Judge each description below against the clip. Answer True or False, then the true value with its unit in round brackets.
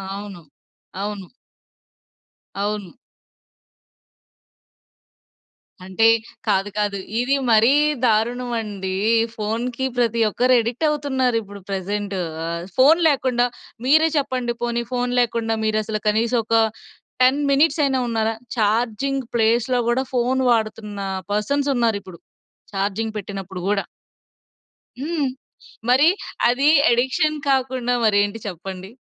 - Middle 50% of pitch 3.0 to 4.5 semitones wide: True (3.7 semitones)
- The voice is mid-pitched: False (230 Hz)